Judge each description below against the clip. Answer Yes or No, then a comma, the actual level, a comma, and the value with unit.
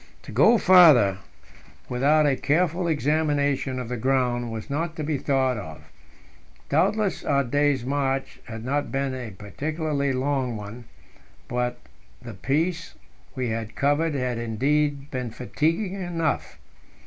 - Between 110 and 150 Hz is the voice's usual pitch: Yes, low, 135 Hz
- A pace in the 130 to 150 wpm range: Yes, slow, 135 wpm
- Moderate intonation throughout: Yes, average, 3.8 semitones